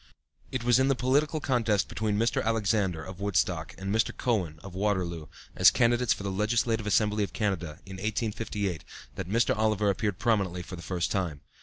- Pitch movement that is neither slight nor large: Yes, average, 3.3 semitones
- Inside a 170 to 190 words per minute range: Yes, average, 180 wpm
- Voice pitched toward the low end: Yes, low, 105 Hz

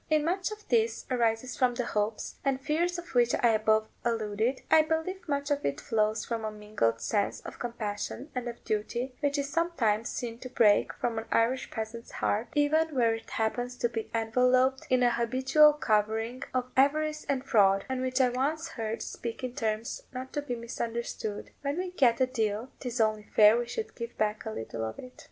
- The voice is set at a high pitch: Yes, high, 240 Hz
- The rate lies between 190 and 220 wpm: Yes, average, 200 wpm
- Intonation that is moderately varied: Yes, average, 3.7 semitones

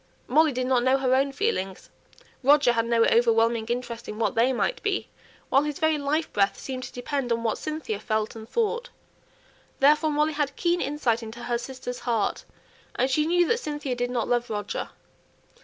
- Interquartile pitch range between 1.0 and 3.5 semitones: No, average, 4.2 semitones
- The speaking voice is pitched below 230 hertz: No, very high, 255 Hz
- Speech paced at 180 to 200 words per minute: Yes, average, 190 wpm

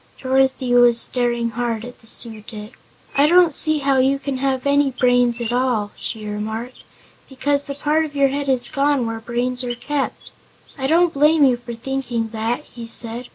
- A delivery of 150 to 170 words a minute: No, average, 190 wpm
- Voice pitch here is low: No, very high, 250 Hz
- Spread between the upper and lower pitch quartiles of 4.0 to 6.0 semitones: No, average, 2.9 semitones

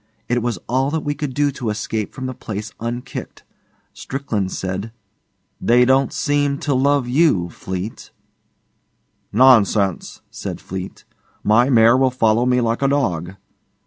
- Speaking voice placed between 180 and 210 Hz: No, low, 120 Hz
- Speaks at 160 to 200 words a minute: No, average, 145 wpm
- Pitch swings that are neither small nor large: Yes, average, 4.1 semitones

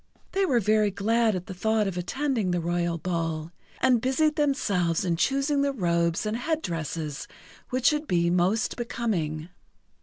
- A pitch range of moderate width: No, wide, 7.0 semitones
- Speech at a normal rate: Yes, average, 160 wpm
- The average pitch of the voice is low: No, high, 200 Hz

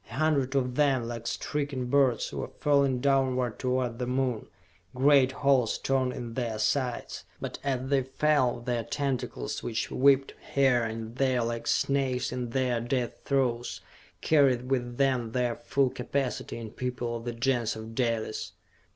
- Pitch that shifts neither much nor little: No, narrow, 2.3 semitones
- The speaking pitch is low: Yes, low, 125 Hz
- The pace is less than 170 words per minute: Yes, average, 155 wpm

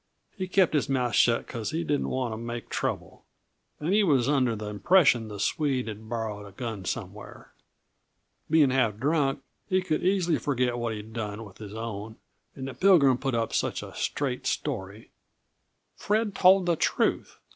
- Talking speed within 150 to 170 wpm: No, average, 180 wpm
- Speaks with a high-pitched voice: No, low, 125 Hz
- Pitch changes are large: Yes, wide, 5.8 semitones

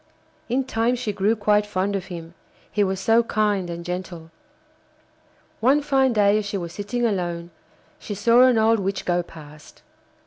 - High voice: Yes, high, 205 Hz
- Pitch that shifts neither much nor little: Yes, average, 4.2 semitones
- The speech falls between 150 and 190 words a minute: Yes, average, 170 wpm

